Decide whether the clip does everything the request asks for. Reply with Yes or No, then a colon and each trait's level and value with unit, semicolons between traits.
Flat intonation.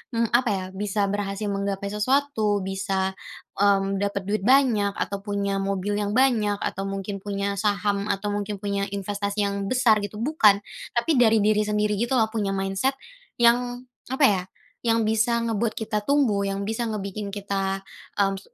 Yes: narrow, 2.0 semitones